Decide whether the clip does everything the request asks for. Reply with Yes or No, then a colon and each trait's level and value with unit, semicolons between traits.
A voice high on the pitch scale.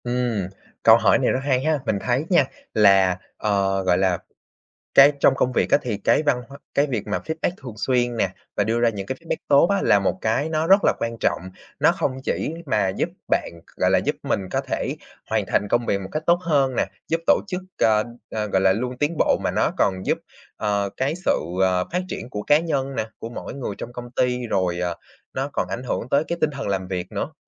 No: low, 120 Hz